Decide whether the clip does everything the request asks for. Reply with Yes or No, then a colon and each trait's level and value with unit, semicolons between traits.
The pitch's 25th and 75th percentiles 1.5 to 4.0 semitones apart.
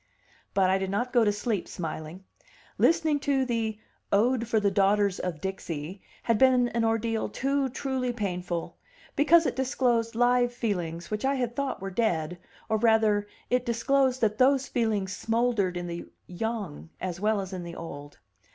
No: average, 4.6 semitones